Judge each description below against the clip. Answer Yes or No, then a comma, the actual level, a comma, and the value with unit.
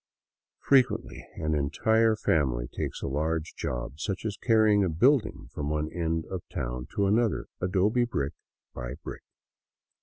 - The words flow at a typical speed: Yes, average, 145 wpm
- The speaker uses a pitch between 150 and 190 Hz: No, very low, 80 Hz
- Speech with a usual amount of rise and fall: No, wide, 7.2 semitones